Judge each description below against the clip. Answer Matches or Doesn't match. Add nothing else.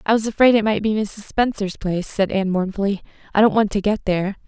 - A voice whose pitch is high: Matches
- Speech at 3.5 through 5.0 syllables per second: Doesn't match